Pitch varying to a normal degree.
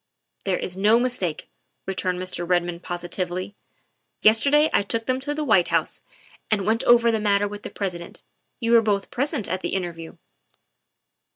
Yes: average, 4.3 semitones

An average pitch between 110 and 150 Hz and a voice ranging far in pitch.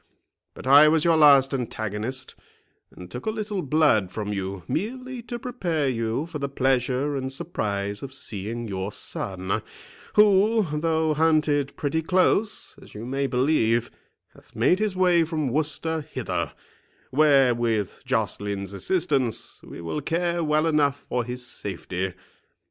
Yes: medium, 140 Hz; wide, 6.1 semitones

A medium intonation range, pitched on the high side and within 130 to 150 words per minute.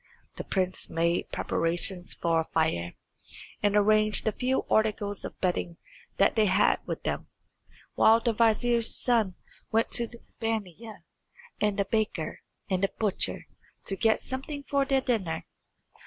Yes: average, 3.8 semitones; high, 210 Hz; average, 145 wpm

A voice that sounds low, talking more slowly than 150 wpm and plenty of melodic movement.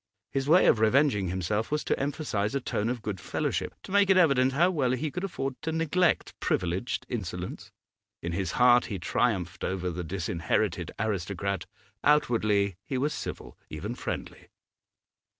No: low, 110 Hz; average, 160 wpm; wide, 7.1 semitones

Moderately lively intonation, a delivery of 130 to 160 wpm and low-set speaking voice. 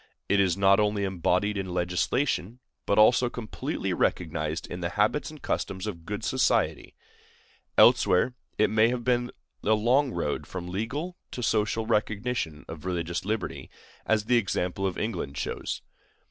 Yes: average, 4.4 semitones; average, 145 wpm; low, 105 Hz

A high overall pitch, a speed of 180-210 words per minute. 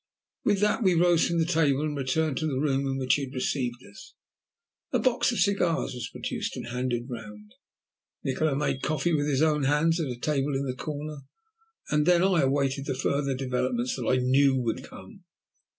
No: medium, 140 Hz; average, 200 wpm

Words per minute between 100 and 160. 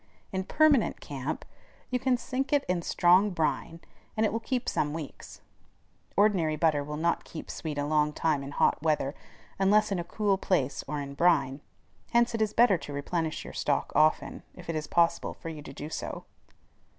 No: average, 190 wpm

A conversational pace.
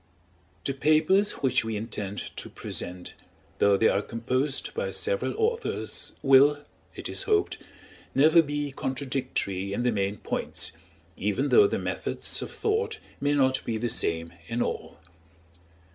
Yes: average, 145 wpm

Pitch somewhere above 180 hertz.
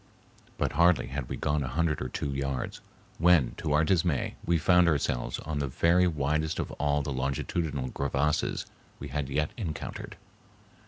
No: very low, 75 Hz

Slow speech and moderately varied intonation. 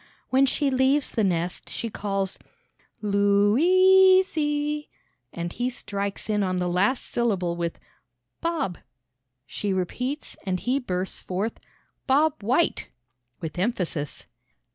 No: slow, 120 wpm; wide, 7.1 semitones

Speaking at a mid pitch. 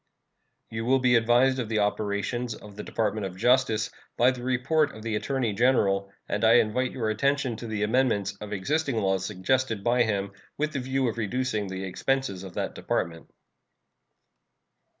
No: low, 115 Hz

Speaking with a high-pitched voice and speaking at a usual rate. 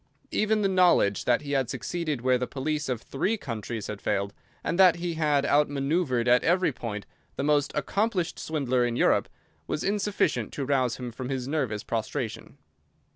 No: medium, 140 Hz; average, 175 wpm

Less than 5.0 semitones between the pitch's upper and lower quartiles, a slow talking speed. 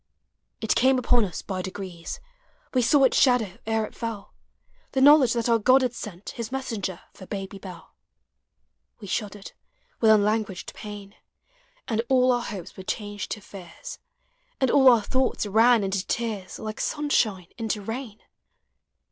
No: average, 3.8 semitones; average, 155 wpm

